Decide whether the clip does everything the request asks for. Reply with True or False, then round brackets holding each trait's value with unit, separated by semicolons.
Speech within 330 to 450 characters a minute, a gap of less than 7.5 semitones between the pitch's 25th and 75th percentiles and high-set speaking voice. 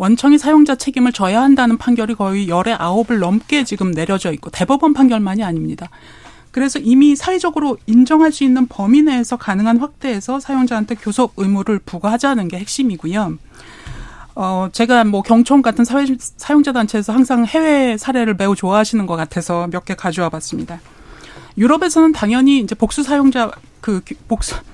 True (375 characters per minute; 5.5 semitones; 230 Hz)